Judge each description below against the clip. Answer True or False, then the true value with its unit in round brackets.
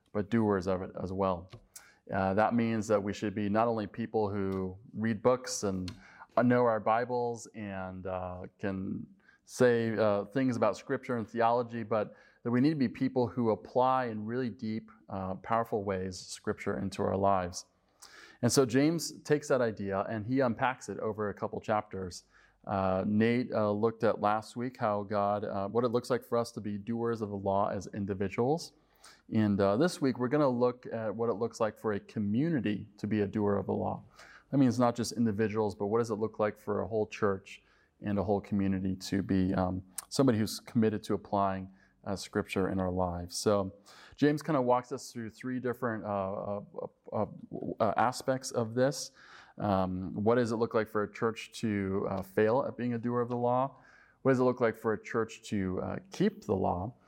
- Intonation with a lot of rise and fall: False (3.5 semitones)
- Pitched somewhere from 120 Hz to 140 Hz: False (110 Hz)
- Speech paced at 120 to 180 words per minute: False (205 wpm)